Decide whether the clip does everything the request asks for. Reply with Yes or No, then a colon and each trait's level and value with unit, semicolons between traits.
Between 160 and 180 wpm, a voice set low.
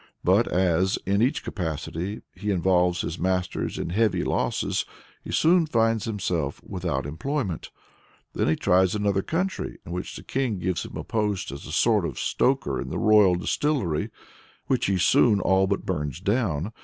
Yes: average, 170 wpm; very low, 95 Hz